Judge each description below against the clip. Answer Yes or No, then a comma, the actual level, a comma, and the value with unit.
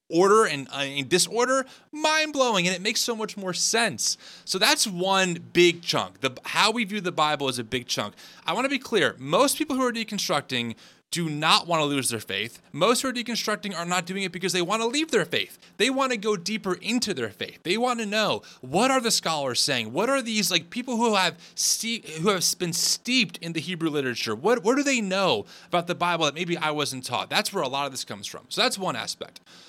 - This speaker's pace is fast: Yes, fast, 240 wpm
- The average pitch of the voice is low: No, high, 190 Hz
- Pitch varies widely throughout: Yes, wide, 6.2 semitones